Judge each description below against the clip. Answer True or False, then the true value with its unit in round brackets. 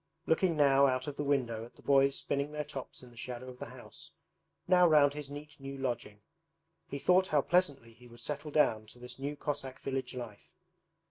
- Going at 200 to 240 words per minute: True (205 wpm)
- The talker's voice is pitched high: False (140 Hz)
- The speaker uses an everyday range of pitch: True (3.0 semitones)